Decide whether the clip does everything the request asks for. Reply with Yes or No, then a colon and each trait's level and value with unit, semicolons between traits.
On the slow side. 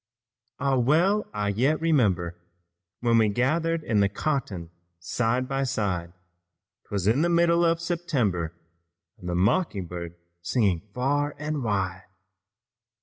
Yes: slow, 130 wpm